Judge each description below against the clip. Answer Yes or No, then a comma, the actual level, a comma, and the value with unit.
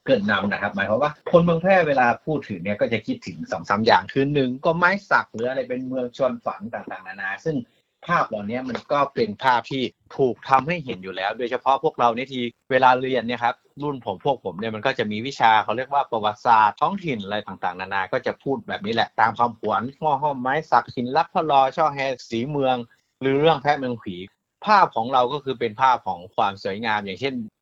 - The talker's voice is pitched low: Yes, low, 130 Hz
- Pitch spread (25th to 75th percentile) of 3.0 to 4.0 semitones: Yes, average, 3.6 semitones